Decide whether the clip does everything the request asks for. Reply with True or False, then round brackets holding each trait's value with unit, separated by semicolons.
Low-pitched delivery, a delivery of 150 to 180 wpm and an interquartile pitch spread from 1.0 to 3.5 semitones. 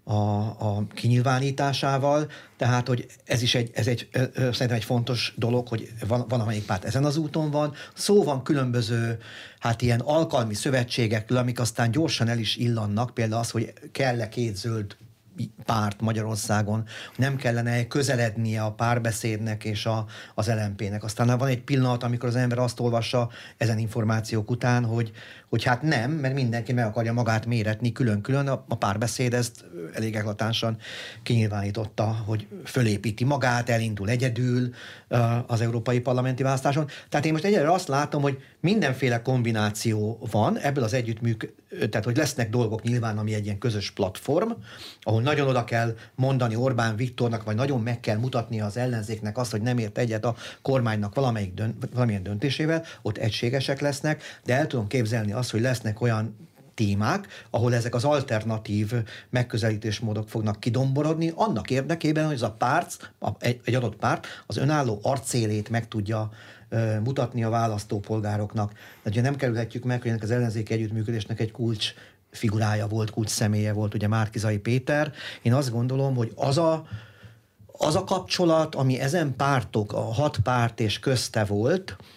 True (120 Hz; 155 wpm; 2.8 semitones)